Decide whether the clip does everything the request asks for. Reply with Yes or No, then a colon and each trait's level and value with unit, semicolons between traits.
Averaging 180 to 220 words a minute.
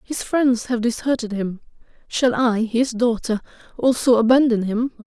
No: average, 140 wpm